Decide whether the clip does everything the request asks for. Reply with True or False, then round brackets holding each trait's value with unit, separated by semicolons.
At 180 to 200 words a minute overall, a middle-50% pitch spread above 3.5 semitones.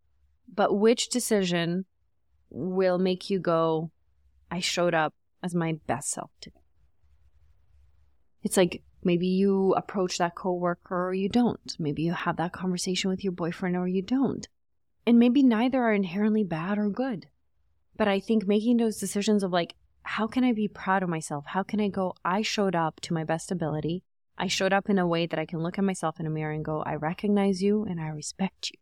True (195 wpm; 4.0 semitones)